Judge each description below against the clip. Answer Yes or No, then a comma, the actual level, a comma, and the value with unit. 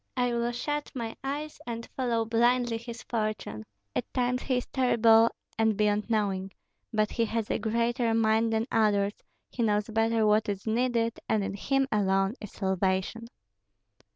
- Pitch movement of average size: No, narrow, 2.1 semitones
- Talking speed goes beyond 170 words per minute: No, average, 160 wpm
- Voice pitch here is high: Yes, high, 225 Hz